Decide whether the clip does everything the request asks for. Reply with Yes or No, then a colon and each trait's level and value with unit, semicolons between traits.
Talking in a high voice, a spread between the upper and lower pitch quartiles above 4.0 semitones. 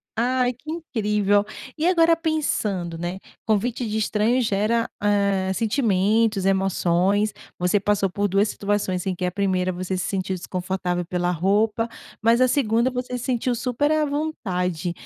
Yes: high, 205 Hz; average, 4.4 semitones